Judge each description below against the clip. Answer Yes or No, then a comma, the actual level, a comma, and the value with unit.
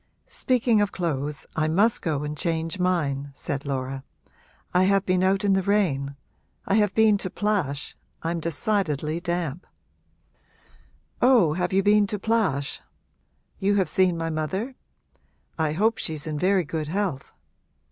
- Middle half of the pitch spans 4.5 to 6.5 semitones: Yes, average, 5.0 semitones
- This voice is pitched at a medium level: Yes, medium, 175 Hz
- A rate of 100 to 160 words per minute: Yes, average, 145 wpm